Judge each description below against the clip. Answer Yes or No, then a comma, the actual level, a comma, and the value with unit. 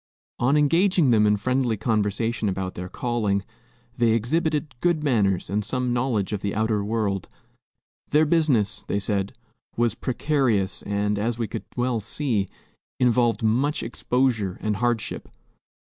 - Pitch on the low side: Yes, low, 115 Hz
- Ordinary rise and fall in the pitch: Yes, average, 3.9 semitones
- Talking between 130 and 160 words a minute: Yes, average, 140 wpm